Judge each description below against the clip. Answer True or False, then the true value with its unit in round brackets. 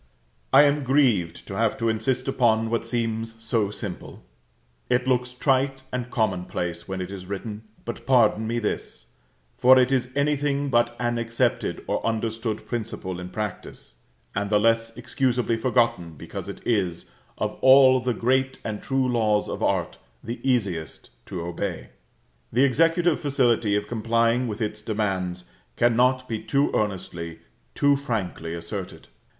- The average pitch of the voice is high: False (115 Hz)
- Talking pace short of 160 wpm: True (150 wpm)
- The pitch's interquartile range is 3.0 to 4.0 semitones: True (3.5 semitones)